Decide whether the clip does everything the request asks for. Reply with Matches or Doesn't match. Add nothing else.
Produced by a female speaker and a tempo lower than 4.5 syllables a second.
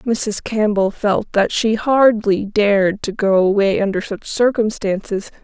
Matches